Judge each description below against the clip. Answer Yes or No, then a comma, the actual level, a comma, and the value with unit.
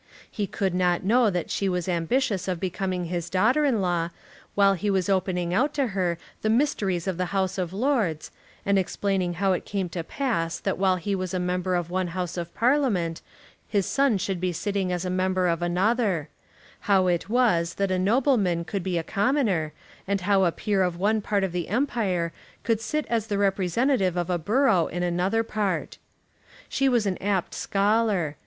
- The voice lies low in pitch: No, high, 190 Hz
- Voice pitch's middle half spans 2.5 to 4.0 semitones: Yes, average, 3.0 semitones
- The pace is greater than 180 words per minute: Yes, average, 195 wpm